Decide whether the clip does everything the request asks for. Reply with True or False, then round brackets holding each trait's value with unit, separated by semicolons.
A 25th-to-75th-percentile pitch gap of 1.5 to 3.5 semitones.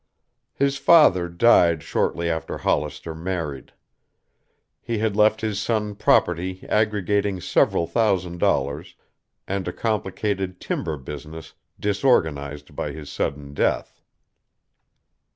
False (4.8 semitones)